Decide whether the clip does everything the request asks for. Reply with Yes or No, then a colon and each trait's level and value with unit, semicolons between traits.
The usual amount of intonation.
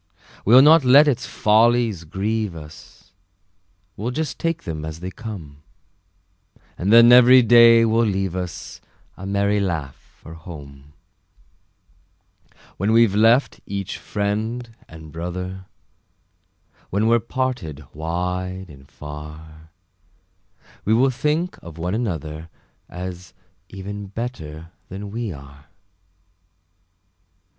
No: wide, 6.2 semitones